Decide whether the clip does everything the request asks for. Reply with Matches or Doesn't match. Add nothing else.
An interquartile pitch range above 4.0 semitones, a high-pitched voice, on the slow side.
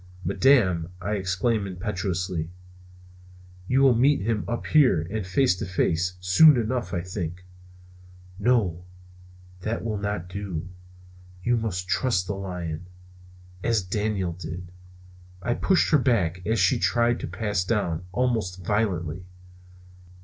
Doesn't match